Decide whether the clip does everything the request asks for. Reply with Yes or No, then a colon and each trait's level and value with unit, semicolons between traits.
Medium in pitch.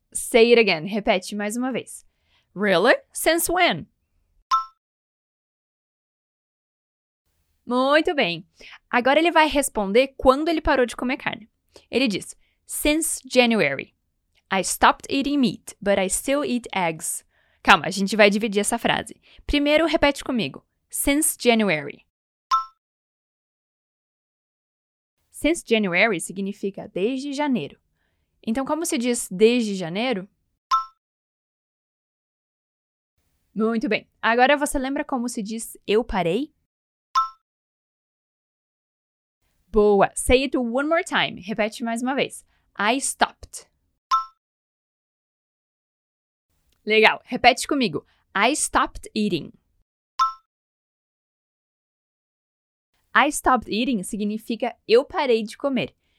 No: high, 245 Hz